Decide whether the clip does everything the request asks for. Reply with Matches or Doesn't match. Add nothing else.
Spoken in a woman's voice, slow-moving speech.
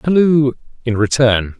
Doesn't match